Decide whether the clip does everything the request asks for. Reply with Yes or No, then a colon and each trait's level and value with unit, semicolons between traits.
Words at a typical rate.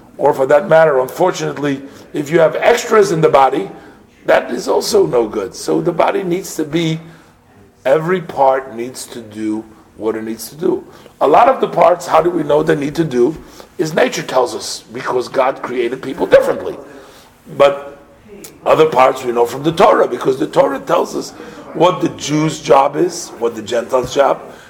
Yes: average, 185 wpm